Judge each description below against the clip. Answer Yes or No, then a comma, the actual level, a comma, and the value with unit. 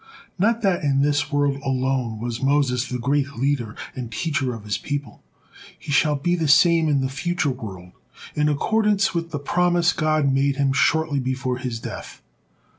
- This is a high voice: No, medium, 140 Hz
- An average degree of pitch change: Yes, average, 3.6 semitones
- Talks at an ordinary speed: Yes, average, 175 wpm